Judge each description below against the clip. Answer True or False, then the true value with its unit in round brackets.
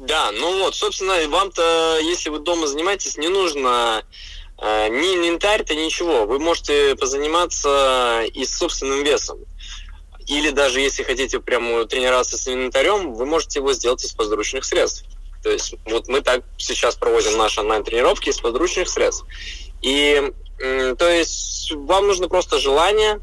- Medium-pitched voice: True (175 Hz)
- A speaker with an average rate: True (150 wpm)